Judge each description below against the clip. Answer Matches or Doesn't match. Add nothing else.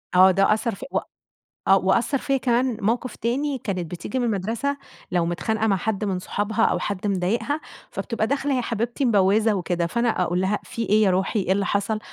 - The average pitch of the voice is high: Matches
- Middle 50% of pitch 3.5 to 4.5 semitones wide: Matches